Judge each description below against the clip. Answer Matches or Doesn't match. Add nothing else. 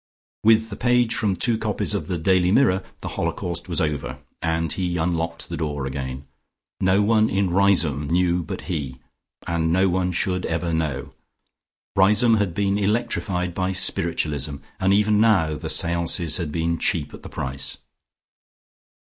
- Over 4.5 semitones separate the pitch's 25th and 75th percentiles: Doesn't match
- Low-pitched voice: Matches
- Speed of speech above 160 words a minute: Doesn't match